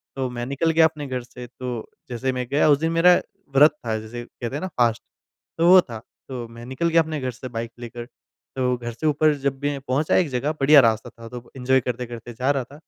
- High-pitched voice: No, low, 130 Hz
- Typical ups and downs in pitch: Yes, average, 3.7 semitones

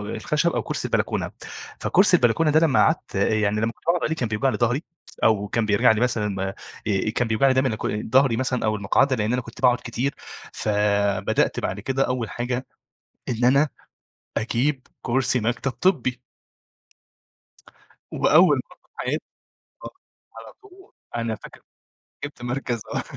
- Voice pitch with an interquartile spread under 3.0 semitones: No, average, 3.5 semitones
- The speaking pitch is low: Yes, low, 120 Hz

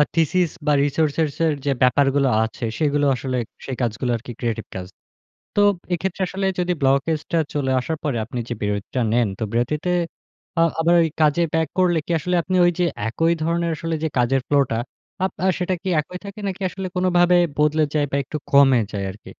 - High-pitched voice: No, medium, 150 Hz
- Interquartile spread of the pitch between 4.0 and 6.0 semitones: Yes, average, 4.7 semitones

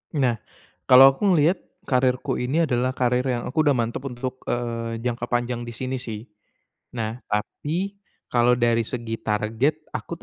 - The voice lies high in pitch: No, low, 125 Hz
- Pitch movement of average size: No, narrow, 2.0 semitones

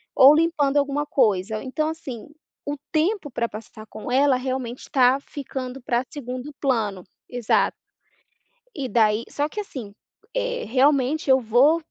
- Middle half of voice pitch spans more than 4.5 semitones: No, average, 3.6 semitones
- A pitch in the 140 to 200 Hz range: No, very high, 265 Hz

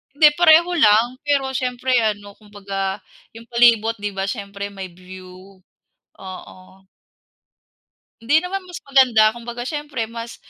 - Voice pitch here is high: Yes, high, 230 Hz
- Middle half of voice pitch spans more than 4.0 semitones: Yes, average, 4.8 semitones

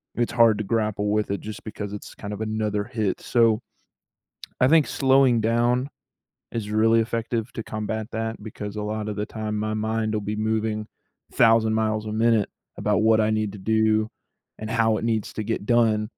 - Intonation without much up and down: Yes, narrow, 1.0 semitones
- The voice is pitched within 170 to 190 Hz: No, low, 110 Hz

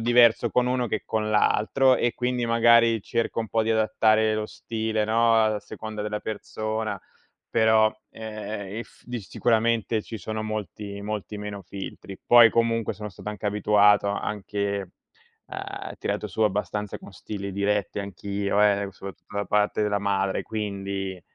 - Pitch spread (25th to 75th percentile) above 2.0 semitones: No, narrow, 1.7 semitones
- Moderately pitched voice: No, low, 105 Hz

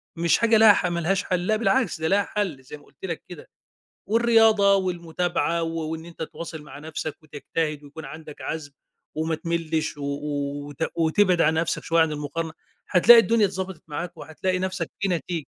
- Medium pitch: Yes, medium, 165 Hz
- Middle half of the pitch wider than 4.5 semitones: No, average, 3.3 semitones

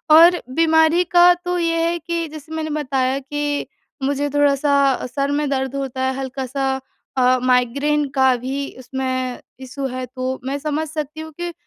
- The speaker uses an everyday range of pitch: Yes, average, 3.2 semitones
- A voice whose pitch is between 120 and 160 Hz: No, very high, 280 Hz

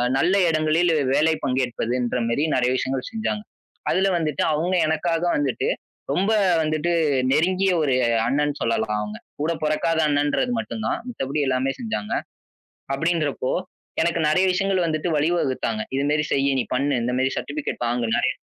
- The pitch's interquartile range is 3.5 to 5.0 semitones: Yes, average, 4.6 semitones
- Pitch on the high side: No, medium, 150 Hz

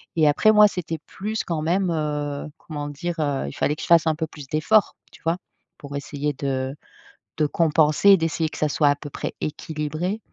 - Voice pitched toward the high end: No, medium, 155 Hz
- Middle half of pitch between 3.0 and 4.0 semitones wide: No, narrow, 2.5 semitones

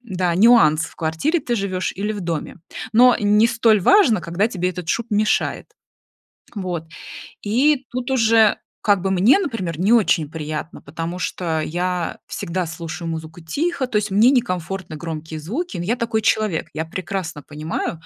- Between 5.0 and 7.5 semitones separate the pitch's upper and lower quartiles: Yes, wide, 5.5 semitones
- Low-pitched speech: No, medium, 185 Hz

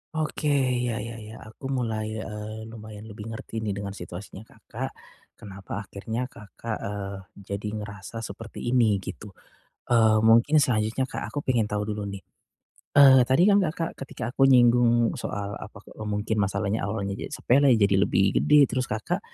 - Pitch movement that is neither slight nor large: Yes, average, 3.0 semitones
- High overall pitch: No, low, 110 Hz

